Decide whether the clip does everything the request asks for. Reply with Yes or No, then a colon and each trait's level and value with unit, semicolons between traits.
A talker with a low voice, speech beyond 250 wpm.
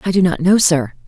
No: medium, 175 Hz; fast, 280 wpm